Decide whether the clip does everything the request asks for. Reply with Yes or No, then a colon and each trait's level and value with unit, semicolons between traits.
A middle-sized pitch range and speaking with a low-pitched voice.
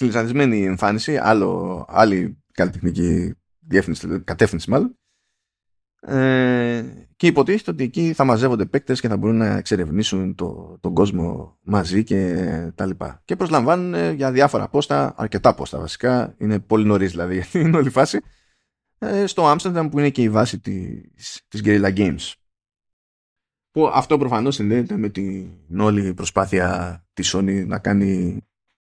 No: wide, 5.8 semitones; low, 105 Hz